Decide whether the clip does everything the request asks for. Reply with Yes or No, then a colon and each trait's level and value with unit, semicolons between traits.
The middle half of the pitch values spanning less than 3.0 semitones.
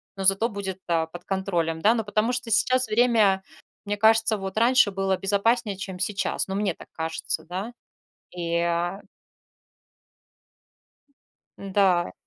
No: average, 3.3 semitones